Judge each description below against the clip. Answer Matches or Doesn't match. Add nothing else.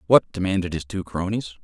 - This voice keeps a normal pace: Matches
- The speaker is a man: Matches